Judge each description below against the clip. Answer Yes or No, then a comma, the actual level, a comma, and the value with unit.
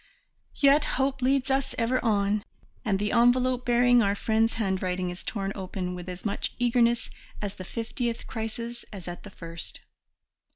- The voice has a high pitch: Yes, high, 225 Hz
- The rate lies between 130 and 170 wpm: Yes, average, 160 wpm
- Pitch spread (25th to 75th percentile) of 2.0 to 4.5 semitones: Yes, average, 4.0 semitones